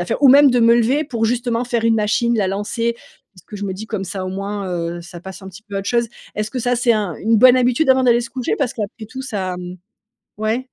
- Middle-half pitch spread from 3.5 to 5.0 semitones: Yes, average, 3.8 semitones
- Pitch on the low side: No, high, 225 Hz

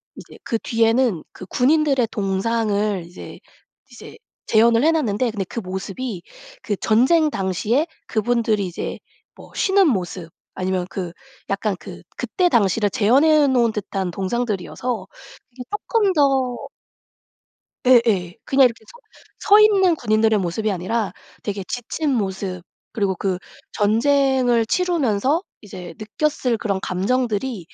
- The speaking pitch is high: Yes, high, 225 Hz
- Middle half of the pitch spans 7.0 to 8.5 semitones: No, average, 5.1 semitones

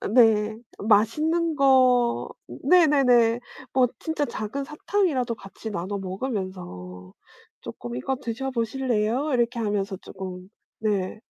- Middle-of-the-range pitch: No, high, 230 Hz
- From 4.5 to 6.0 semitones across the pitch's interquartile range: Yes, average, 5.1 semitones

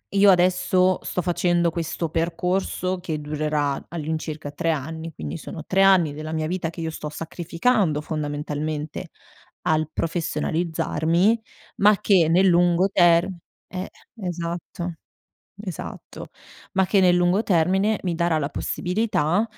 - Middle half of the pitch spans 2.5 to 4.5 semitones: Yes, average, 2.8 semitones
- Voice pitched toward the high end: No, medium, 170 Hz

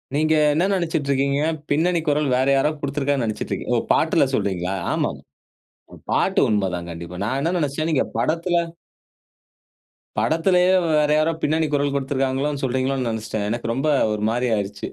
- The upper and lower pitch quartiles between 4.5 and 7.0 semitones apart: Yes, average, 5.0 semitones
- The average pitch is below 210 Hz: Yes, medium, 140 Hz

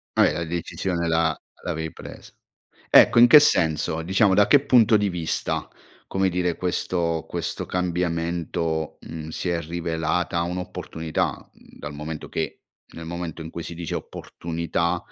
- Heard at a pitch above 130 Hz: No, very low, 85 Hz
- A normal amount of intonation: No, narrow, 1.9 semitones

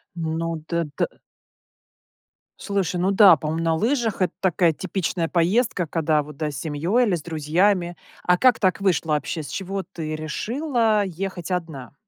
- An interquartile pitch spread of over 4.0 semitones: No, average, 3.7 semitones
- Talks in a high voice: No, medium, 175 Hz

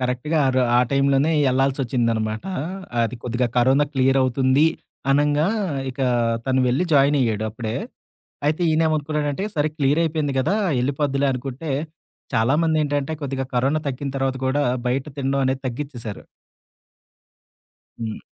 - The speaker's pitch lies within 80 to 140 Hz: Yes, low, 135 Hz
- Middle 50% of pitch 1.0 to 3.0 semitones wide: Yes, narrow, 2.6 semitones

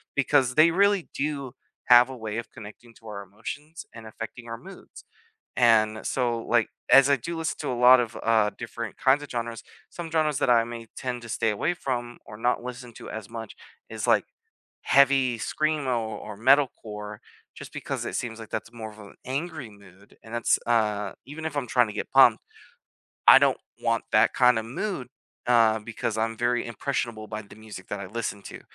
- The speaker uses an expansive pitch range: No, average, 3.3 semitones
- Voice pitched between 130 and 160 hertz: No, low, 120 Hz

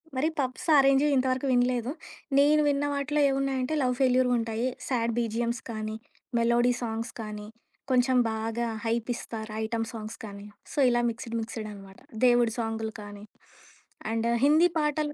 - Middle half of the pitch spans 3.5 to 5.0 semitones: No, average, 2.7 semitones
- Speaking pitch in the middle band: No, high, 235 Hz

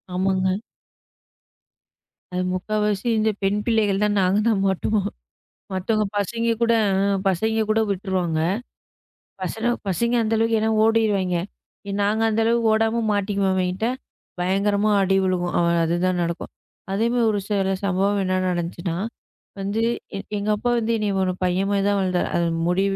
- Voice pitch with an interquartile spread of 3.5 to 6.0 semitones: No, average, 2.8 semitones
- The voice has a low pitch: No, high, 200 Hz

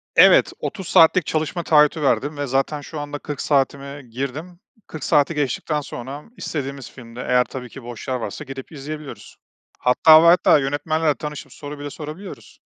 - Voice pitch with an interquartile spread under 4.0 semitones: Yes, narrow, 2.4 semitones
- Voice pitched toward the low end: No, medium, 145 Hz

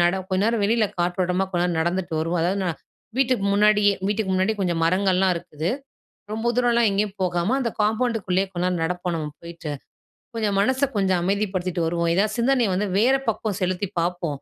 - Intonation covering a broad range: No, average, 3.3 semitones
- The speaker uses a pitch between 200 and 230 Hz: No, high, 190 Hz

